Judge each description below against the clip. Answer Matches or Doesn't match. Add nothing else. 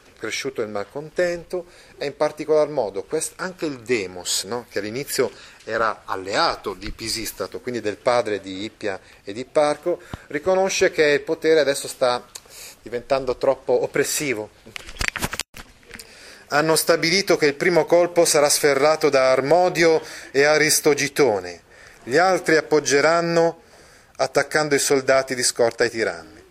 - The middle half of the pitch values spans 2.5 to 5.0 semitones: Matches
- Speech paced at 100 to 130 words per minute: Matches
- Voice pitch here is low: Doesn't match